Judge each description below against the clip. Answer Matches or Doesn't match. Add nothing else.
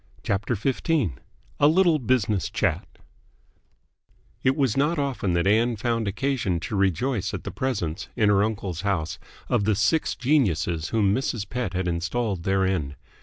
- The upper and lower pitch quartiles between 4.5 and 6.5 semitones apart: Matches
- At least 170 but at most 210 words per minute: Doesn't match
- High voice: Doesn't match